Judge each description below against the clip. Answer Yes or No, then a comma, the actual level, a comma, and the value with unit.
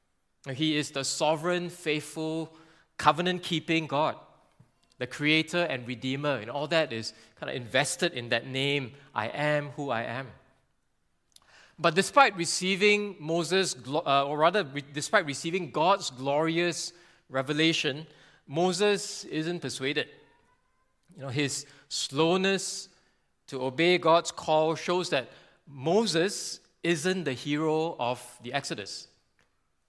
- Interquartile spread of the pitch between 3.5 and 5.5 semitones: Yes, average, 4.3 semitones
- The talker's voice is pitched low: No, medium, 155 Hz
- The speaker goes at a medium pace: No, slow, 115 wpm